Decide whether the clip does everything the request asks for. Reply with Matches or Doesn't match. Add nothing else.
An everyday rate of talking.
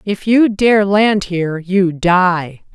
Matches